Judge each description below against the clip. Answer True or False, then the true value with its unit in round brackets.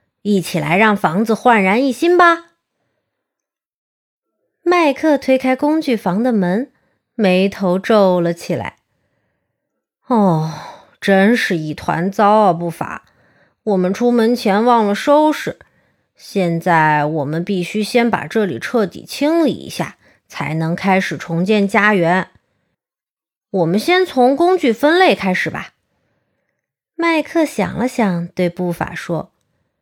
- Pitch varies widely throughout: True (6.0 semitones)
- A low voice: False (205 Hz)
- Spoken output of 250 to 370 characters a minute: False (175 characters per minute)